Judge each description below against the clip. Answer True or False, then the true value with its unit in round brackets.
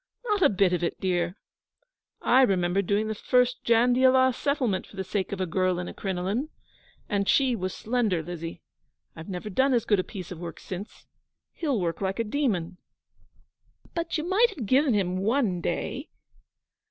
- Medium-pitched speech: False (205 Hz)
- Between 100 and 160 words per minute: False (175 wpm)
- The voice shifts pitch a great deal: True (5.8 semitones)